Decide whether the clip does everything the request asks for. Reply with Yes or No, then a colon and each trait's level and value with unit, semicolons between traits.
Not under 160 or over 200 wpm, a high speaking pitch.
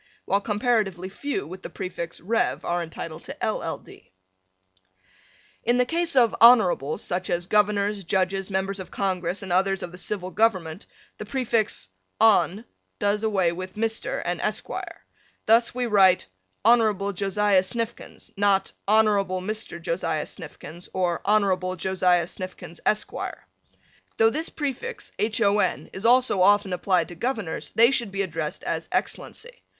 No: average, 145 wpm; high, 195 Hz